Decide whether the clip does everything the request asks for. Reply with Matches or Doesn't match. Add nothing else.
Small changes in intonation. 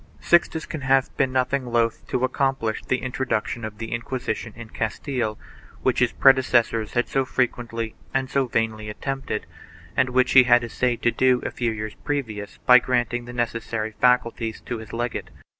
Matches